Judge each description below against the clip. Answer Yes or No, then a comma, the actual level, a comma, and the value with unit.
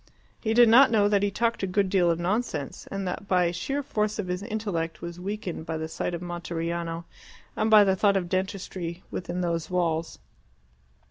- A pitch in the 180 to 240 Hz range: Yes, medium, 185 Hz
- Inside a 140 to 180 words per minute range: No, average, 195 wpm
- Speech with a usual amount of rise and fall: Yes, average, 3.4 semitones